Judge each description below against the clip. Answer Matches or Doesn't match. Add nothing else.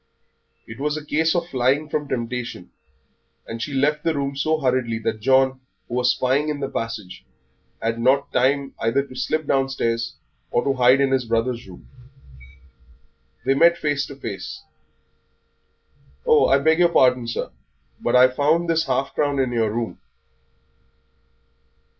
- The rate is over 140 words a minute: Matches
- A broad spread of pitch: Doesn't match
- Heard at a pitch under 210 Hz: Matches